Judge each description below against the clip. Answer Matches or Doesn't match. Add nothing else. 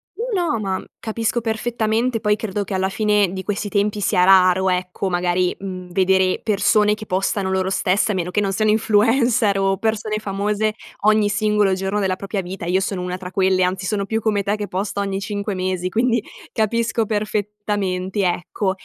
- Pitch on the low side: Doesn't match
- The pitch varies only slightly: Matches